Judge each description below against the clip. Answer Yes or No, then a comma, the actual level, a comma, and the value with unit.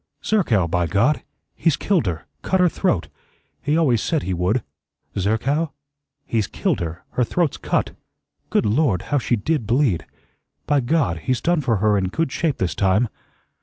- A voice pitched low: Yes, low, 120 Hz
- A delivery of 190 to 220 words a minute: No, average, 165 wpm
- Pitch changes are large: Yes, wide, 8.0 semitones